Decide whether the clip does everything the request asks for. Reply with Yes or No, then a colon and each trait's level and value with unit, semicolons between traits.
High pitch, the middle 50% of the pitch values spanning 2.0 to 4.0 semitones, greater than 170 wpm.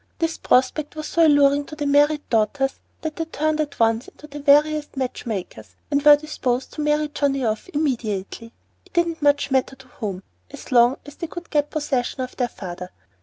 Yes: very high, 285 Hz; average, 3.6 semitones; average, 195 wpm